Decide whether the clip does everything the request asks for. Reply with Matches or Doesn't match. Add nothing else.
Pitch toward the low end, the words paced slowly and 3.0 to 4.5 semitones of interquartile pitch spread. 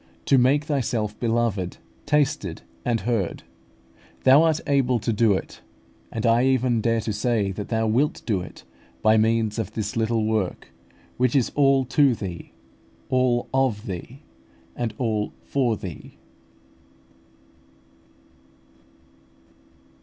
Matches